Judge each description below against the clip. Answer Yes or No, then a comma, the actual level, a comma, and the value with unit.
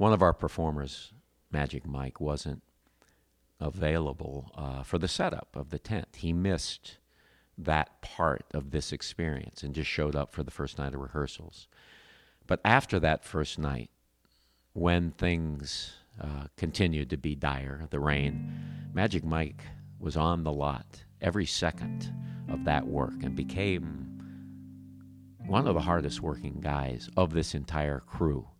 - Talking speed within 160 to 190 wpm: No, average, 145 wpm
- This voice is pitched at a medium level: No, very low, 75 Hz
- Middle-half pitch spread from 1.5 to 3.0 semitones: No, average, 3.5 semitones